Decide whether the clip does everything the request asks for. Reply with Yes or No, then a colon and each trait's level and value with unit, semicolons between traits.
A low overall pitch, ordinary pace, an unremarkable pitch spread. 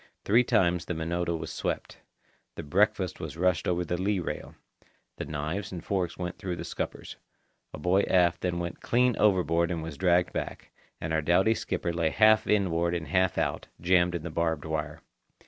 No: very low, 85 Hz; average, 180 wpm; narrow, 2.0 semitones